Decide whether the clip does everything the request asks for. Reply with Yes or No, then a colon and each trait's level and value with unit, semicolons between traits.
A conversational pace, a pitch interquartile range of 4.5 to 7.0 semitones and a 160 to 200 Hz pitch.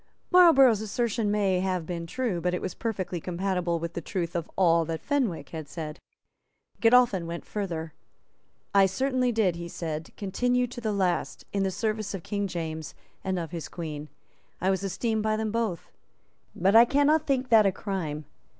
Yes: average, 175 wpm; average, 4.8 semitones; high, 190 Hz